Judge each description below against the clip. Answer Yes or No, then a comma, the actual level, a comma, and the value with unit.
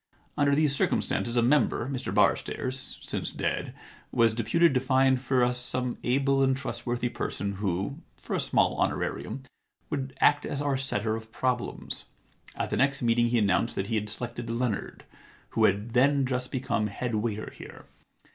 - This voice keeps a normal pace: Yes, average, 165 wpm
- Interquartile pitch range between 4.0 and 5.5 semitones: No, average, 2.7 semitones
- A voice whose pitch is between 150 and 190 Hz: No, low, 125 Hz